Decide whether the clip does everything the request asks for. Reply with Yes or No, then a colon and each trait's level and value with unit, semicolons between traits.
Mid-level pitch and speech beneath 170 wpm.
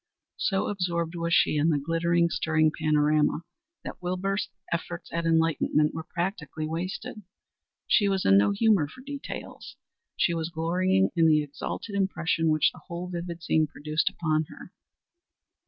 Yes: medium, 170 Hz; average, 150 wpm